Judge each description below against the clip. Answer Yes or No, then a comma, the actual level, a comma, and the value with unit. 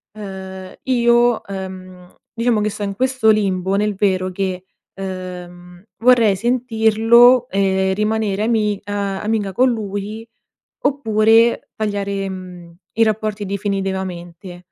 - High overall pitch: Yes, high, 200 Hz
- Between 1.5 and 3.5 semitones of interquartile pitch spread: Yes, average, 2.7 semitones